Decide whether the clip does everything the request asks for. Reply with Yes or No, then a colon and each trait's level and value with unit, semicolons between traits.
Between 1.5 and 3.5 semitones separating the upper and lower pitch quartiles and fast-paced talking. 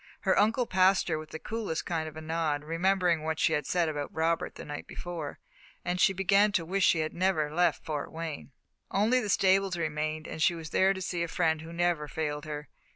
Yes: average, 3.2 semitones; fast, 220 wpm